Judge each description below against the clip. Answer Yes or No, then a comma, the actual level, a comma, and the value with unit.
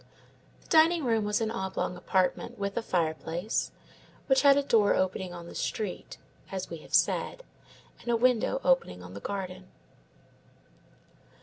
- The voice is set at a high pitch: Yes, high, 200 Hz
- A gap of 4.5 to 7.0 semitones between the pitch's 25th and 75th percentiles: Yes, average, 4.8 semitones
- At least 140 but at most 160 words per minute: Yes, average, 150 wpm